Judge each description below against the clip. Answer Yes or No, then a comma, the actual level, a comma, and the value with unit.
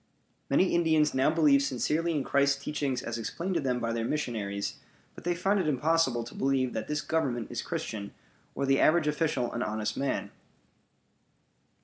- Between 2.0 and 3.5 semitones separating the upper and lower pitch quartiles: No, average, 4.7 semitones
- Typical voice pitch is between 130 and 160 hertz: Yes, medium, 140 Hz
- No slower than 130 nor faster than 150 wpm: No, average, 170 wpm